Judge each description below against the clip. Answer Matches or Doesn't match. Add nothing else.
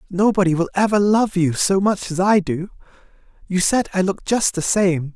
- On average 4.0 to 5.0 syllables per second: Doesn't match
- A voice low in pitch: Doesn't match